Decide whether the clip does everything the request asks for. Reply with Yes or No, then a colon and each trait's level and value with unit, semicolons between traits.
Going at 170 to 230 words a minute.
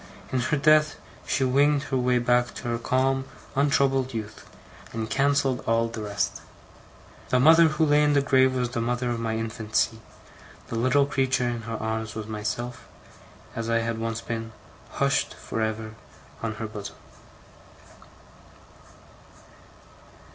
No: average, 145 wpm